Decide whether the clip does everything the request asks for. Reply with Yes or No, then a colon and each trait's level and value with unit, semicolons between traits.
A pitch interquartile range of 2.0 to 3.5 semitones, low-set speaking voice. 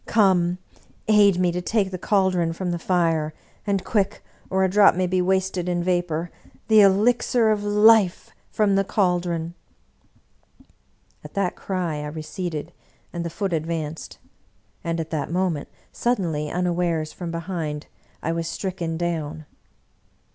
No: average, 2.7 semitones; medium, 180 Hz